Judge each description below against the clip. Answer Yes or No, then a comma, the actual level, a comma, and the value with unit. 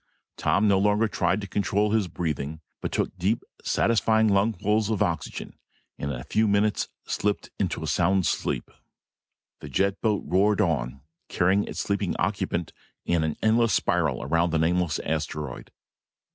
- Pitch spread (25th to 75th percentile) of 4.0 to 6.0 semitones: Yes, average, 4.3 semitones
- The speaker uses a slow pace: No, average, 155 wpm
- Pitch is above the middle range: No, very low, 95 Hz